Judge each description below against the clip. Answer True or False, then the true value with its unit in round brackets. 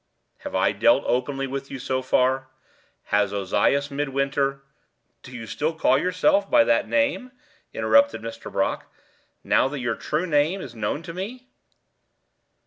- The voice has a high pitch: False (140 Hz)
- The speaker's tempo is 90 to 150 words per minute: True (145 wpm)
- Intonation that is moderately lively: False (6.0 semitones)